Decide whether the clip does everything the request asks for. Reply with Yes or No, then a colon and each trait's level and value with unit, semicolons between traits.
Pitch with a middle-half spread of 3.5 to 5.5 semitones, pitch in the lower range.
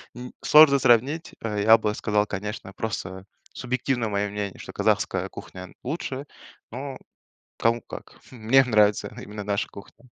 Yes: average, 3.8 semitones; low, 110 Hz